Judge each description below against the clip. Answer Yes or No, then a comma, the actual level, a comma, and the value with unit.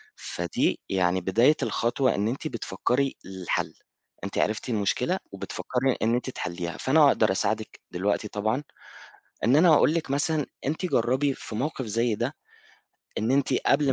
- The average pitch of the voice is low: Yes, low, 120 Hz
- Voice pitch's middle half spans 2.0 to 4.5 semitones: No, average, 5.3 semitones